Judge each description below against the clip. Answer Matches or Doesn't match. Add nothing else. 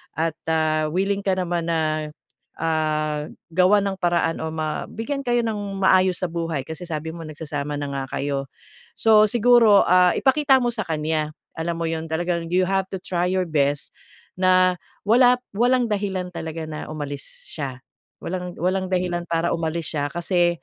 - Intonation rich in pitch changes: Doesn't match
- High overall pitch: Doesn't match